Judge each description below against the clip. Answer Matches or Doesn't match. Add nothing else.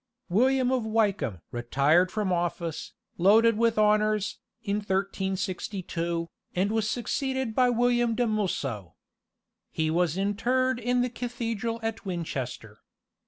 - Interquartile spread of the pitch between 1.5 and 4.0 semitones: Doesn't match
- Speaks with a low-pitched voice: Doesn't match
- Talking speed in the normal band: Doesn't match